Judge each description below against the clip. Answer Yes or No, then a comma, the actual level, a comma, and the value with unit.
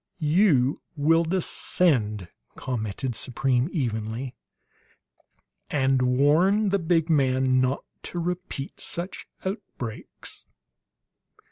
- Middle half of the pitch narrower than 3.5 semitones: No, average, 5.3 semitones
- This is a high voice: No, medium, 140 Hz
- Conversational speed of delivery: No, slow, 85 wpm